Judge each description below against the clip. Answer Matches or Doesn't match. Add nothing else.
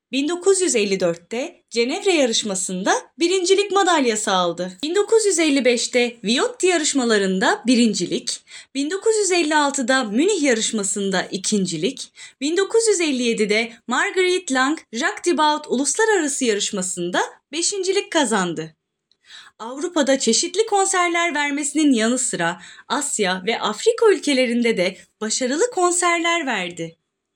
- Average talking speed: Doesn't match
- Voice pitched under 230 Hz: Doesn't match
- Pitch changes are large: Matches